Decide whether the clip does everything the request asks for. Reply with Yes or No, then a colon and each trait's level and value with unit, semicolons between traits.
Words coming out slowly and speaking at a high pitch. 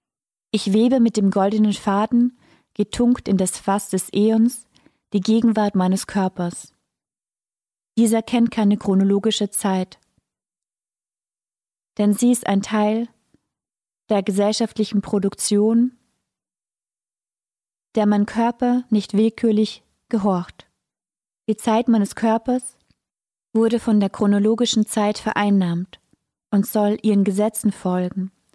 Yes: slow, 105 wpm; high, 210 Hz